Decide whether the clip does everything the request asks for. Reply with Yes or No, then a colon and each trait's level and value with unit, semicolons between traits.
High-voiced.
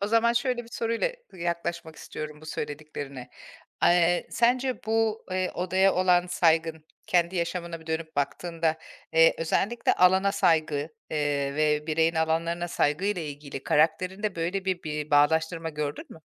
No: medium, 165 Hz